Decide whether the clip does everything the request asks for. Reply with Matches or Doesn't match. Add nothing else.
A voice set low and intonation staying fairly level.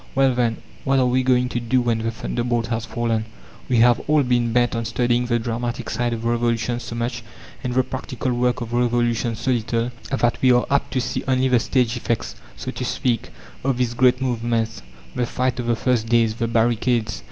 Matches